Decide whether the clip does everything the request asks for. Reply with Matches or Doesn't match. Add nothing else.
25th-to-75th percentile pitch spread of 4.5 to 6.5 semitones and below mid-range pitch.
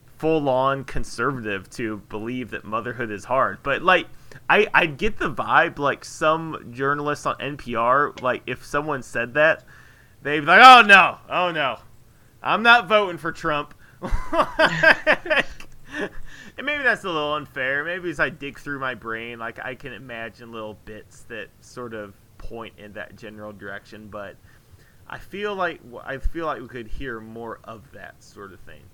Matches